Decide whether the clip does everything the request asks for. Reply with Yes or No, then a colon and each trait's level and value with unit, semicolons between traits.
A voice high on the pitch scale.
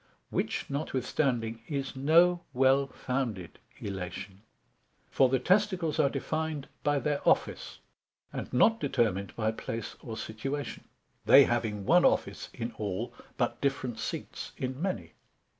No: low, 130 Hz